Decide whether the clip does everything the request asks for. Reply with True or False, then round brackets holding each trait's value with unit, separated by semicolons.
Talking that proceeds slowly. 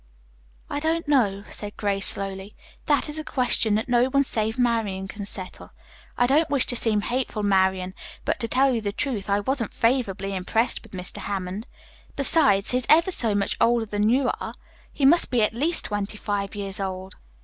False (195 wpm)